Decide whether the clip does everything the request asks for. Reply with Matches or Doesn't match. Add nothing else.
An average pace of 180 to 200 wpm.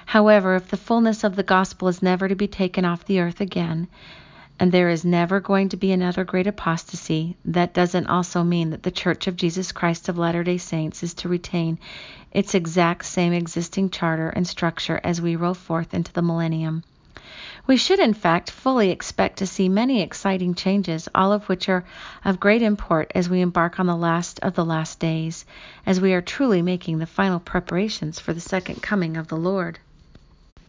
Matches